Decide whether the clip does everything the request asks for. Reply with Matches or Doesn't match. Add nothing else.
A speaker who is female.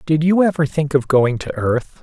Doesn't match